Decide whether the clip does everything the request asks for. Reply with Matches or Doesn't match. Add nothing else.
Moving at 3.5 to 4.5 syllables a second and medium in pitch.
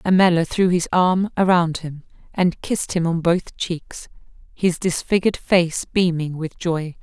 Matches